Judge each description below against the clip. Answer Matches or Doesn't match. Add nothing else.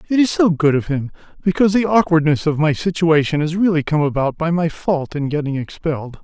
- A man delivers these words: Matches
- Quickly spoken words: Matches